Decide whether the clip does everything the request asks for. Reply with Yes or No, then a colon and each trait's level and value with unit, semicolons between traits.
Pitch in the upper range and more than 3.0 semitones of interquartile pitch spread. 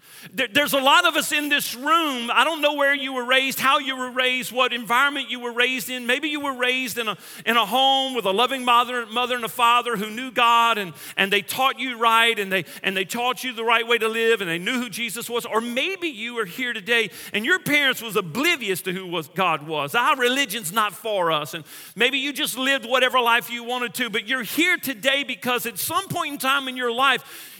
No: high, 245 Hz; average, 2.7 semitones